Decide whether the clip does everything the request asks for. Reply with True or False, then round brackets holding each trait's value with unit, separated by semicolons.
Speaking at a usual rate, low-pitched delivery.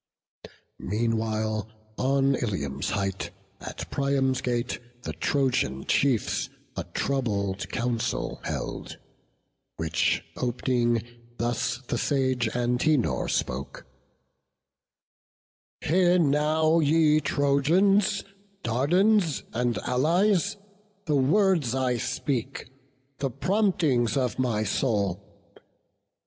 False (85 wpm; 130 Hz)